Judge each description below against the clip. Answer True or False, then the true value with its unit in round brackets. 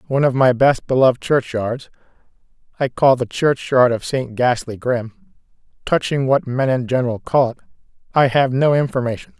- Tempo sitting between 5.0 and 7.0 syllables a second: True (5.1 syllables/s)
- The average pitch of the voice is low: True (130 Hz)